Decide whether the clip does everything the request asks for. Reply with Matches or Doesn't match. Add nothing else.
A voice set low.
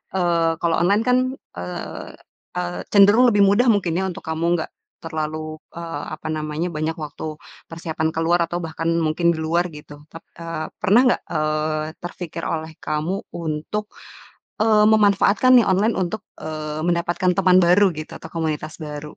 Doesn't match